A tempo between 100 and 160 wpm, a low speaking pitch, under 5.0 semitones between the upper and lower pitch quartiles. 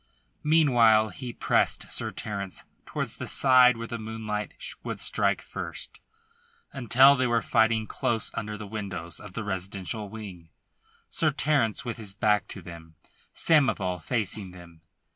Yes: average, 140 wpm; low, 110 Hz; average, 3.5 semitones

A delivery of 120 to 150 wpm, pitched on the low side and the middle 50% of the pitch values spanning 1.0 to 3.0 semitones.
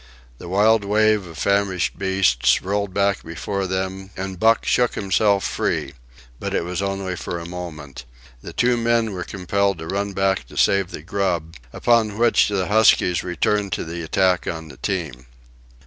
No: average, 170 wpm; very low, 95 Hz; narrow, 2.4 semitones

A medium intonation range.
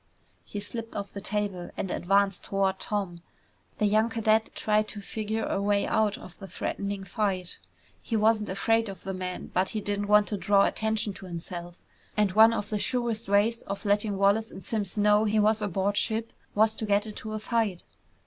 No: narrow, 1.8 semitones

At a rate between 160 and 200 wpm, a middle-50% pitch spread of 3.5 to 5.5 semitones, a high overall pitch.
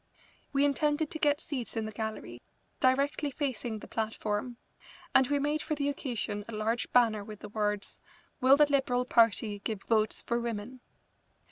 Yes: average, 165 wpm; average, 4.6 semitones; high, 240 Hz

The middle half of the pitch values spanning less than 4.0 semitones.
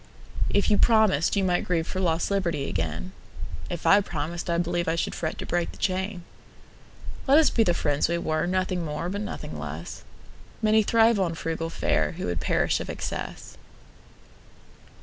Yes: average, 3.5 semitones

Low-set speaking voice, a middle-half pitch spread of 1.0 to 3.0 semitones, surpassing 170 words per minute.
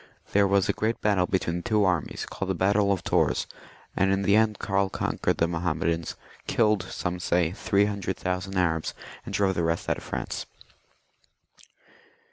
Yes: very low, 95 Hz; narrow, 2.4 semitones; average, 180 wpm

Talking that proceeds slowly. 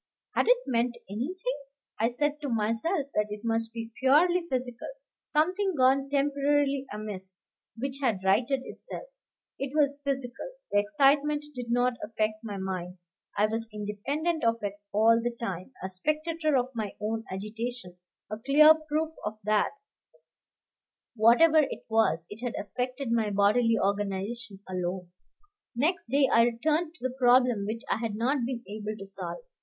No: average, 150 wpm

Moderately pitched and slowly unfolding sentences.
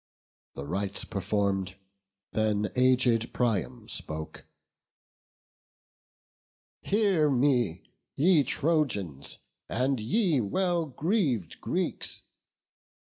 No: low, 120 Hz; slow, 75 wpm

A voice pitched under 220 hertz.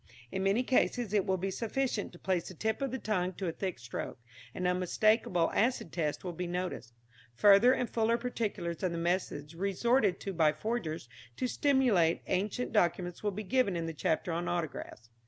Yes: high, 190 Hz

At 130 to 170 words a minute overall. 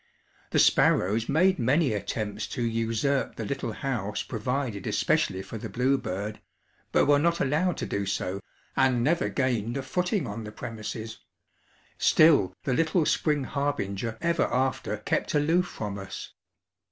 Yes: average, 145 wpm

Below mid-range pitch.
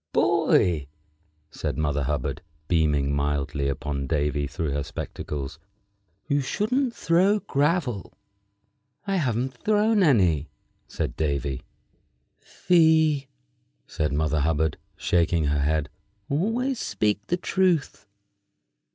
Yes: very low, 85 Hz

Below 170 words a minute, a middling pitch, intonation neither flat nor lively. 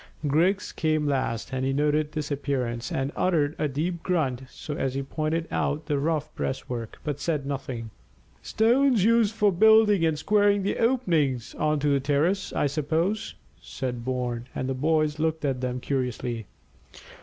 Yes: average, 160 wpm; medium, 150 Hz; average, 4.1 semitones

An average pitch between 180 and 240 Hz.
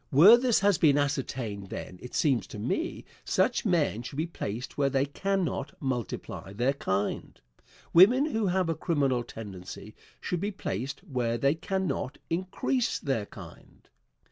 No: medium, 140 Hz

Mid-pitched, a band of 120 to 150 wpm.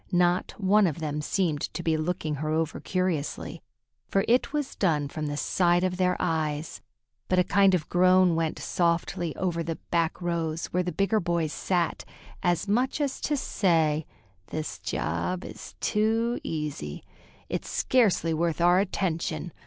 No: medium, 175 Hz; average, 160 wpm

